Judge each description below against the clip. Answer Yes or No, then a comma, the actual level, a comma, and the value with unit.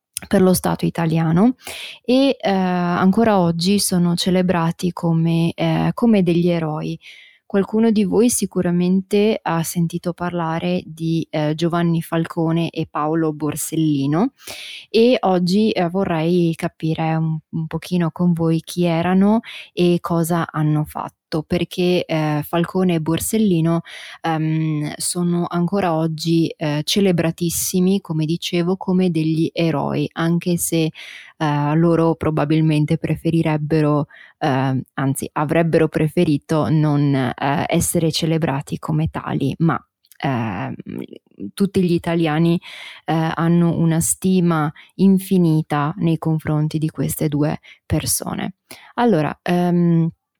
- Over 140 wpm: No, slow, 115 wpm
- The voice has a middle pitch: Yes, medium, 165 Hz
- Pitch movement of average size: No, narrow, 2.1 semitones